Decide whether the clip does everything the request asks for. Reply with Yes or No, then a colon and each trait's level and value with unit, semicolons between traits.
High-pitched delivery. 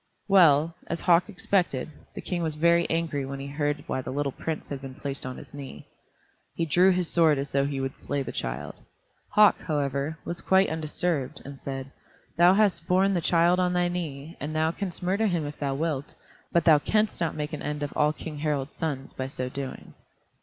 No: medium, 155 Hz